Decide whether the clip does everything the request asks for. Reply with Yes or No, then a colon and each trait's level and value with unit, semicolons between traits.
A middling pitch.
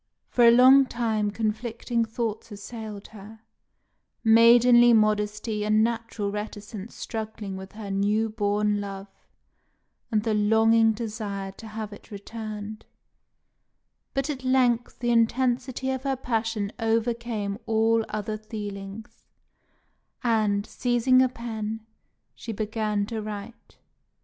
No: high, 220 Hz